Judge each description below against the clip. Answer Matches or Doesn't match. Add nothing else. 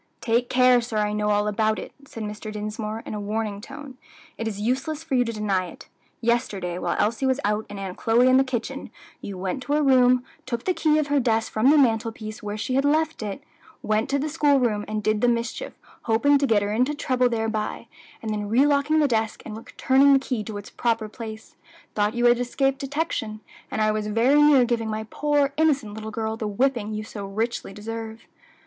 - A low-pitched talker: Doesn't match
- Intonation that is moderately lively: Matches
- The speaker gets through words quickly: Matches